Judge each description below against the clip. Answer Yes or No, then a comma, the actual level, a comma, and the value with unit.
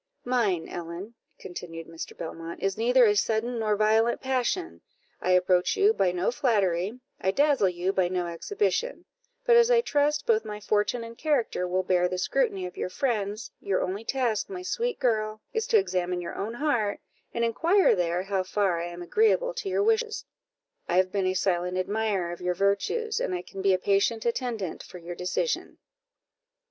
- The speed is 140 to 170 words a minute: No, average, 185 wpm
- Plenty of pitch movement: Yes, wide, 6.0 semitones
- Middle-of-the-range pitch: No, high, 210 Hz